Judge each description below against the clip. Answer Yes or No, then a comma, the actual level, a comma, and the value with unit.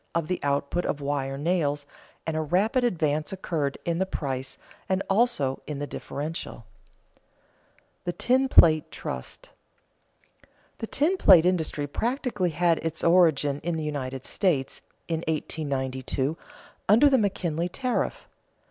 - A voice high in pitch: No, medium, 160 Hz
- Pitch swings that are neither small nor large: Yes, average, 4.5 semitones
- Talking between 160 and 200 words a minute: No, slow, 135 wpm